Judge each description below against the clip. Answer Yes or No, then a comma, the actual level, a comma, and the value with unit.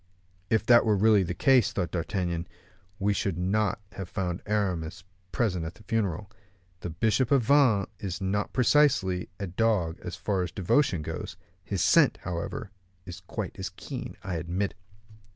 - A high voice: No, very low, 95 Hz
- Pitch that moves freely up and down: No, average, 3.6 semitones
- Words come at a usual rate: Yes, average, 160 wpm